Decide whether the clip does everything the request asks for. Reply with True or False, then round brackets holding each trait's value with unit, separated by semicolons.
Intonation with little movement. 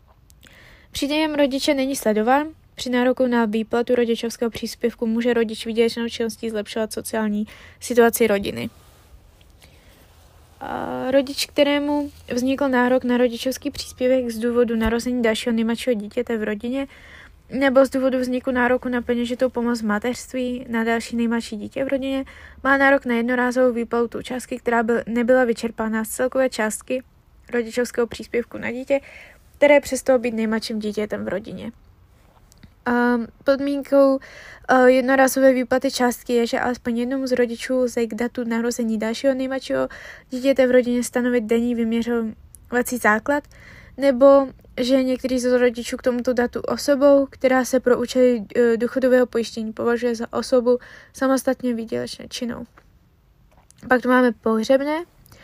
True (2.0 semitones)